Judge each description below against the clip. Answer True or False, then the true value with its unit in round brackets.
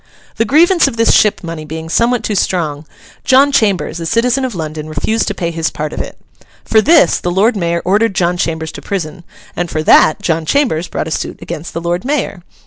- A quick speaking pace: True (215 wpm)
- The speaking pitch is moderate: True (180 Hz)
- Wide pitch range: True (5.9 semitones)